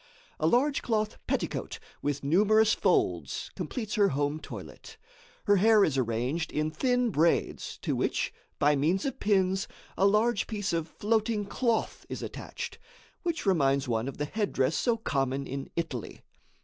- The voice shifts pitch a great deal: Yes, wide, 7.1 semitones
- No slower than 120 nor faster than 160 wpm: Yes, average, 150 wpm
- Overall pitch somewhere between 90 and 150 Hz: No, high, 190 Hz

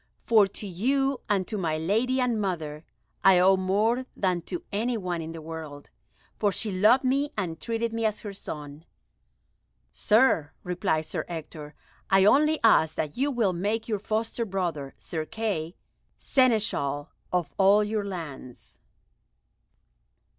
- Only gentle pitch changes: No, wide, 5.6 semitones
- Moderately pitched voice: No, high, 195 Hz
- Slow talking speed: No, average, 145 wpm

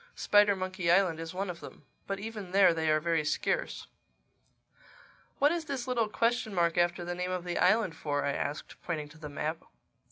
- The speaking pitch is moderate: Yes, medium, 180 Hz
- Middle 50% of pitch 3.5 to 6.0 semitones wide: Yes, average, 4.1 semitones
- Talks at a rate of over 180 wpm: Yes, average, 190 wpm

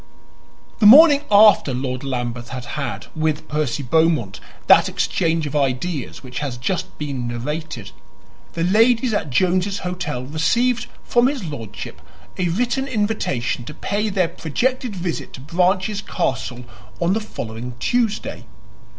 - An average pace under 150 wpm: Yes, slow, 135 wpm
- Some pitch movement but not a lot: No, wide, 8.2 semitones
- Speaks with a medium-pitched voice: Yes, medium, 165 Hz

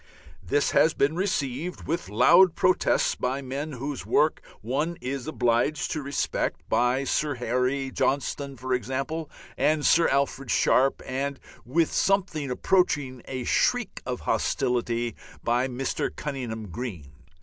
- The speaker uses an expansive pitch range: No, average, 3.4 semitones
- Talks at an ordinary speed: No, slow, 130 wpm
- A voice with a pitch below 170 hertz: Yes, low, 135 Hz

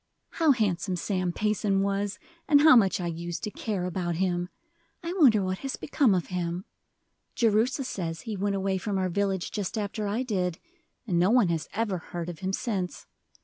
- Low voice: No, high, 195 Hz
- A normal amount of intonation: Yes, average, 3.3 semitones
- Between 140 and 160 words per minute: No, average, 190 wpm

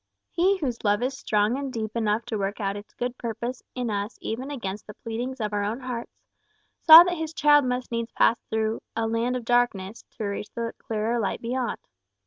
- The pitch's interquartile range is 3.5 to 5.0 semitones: No, average, 2.9 semitones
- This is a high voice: Yes, high, 230 Hz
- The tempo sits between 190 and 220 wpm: Yes, fast, 205 wpm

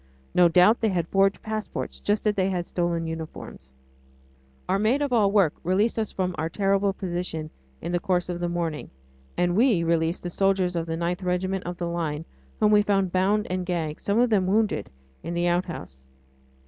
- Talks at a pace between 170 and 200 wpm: Yes, average, 195 wpm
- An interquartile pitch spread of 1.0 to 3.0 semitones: Yes, average, 2.7 semitones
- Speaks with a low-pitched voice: No, medium, 180 Hz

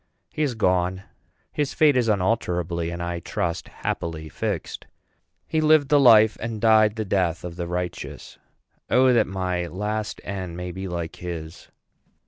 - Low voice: Yes, very low, 95 Hz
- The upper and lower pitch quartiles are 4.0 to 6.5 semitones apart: Yes, average, 4.4 semitones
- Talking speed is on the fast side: No, average, 155 wpm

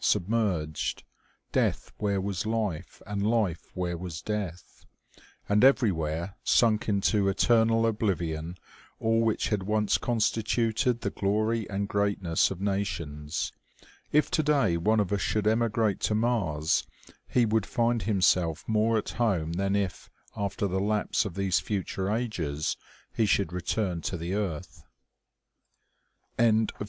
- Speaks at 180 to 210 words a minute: No, slow, 135 wpm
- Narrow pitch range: No, average, 3.7 semitones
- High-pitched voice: No, low, 100 Hz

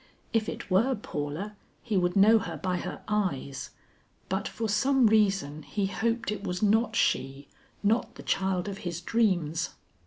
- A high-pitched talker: Yes, high, 200 Hz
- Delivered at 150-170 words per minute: Yes, average, 160 wpm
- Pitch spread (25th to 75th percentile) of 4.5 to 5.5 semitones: No, average, 3.6 semitones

